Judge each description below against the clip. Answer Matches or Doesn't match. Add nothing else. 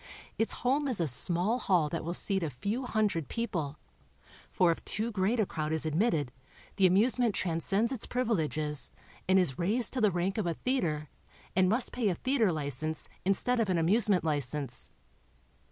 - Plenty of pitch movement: Matches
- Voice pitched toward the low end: Doesn't match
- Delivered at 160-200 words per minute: Matches